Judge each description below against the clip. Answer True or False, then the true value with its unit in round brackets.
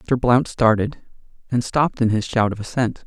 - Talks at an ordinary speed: True (195 wpm)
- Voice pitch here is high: False (115 Hz)